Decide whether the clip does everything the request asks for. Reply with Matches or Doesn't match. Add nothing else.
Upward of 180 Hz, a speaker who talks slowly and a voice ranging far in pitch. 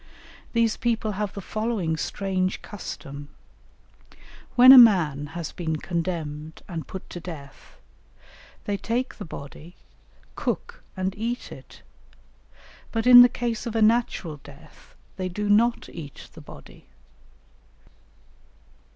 Matches